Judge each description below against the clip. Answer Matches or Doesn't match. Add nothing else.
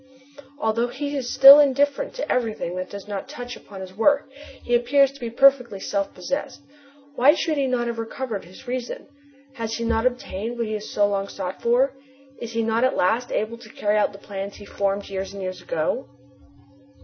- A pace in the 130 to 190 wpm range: Doesn't match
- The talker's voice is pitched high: Matches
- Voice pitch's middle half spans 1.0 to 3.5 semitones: Doesn't match